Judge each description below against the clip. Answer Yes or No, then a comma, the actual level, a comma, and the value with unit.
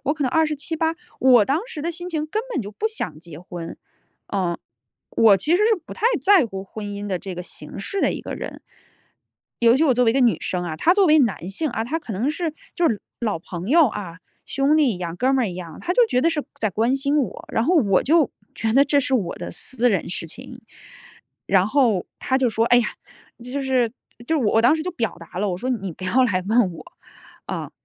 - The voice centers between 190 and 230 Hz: No, high, 245 Hz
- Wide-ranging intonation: Yes, wide, 7.5 semitones